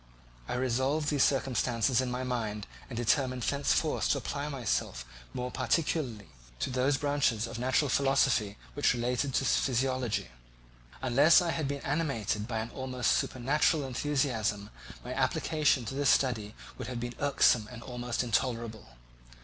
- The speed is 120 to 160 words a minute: Yes, average, 145 wpm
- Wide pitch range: No, average, 3.1 semitones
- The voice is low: Yes, low, 125 Hz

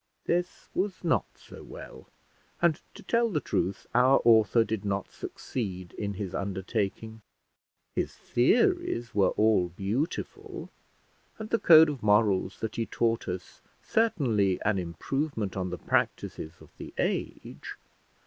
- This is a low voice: Yes, low, 110 Hz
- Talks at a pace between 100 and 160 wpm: Yes, slow, 135 wpm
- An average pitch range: No, wide, 7.3 semitones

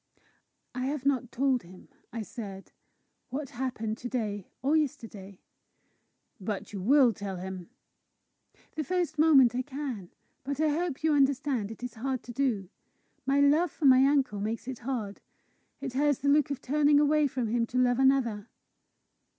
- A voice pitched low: No, very high, 255 Hz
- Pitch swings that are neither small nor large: Yes, average, 4.3 semitones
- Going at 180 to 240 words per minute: No, average, 165 wpm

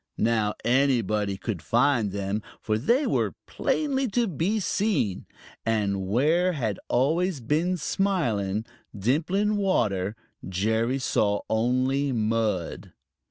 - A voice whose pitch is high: No, low, 120 Hz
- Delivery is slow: Yes, slow, 110 wpm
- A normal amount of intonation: No, wide, 8.4 semitones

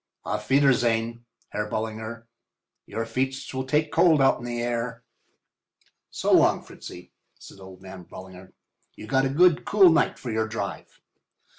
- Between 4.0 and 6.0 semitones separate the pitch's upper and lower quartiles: No, average, 3.6 semitones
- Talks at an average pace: Yes, average, 150 wpm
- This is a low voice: Yes, low, 115 Hz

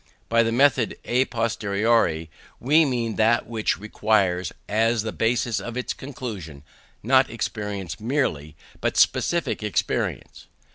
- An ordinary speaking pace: No, slow, 125 wpm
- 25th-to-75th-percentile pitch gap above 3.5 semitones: No, average, 2.9 semitones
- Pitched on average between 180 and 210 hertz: No, low, 115 Hz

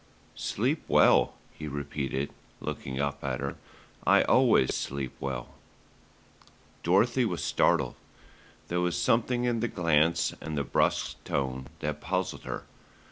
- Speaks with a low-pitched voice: Yes, very low, 75 Hz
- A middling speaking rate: No, slow, 130 wpm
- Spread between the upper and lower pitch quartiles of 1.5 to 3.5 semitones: No, average, 4.4 semitones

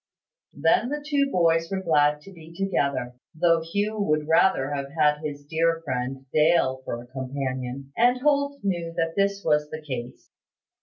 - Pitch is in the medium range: Yes, medium, 160 Hz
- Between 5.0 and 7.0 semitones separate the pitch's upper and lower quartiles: Yes, wide, 5.5 semitones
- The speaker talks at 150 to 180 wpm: Yes, average, 165 wpm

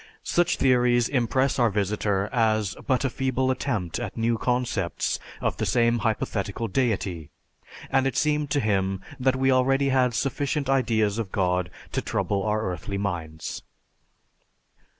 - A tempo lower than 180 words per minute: Yes, average, 145 wpm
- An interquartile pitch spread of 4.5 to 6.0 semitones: Yes, average, 4.8 semitones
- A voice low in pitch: Yes, low, 115 Hz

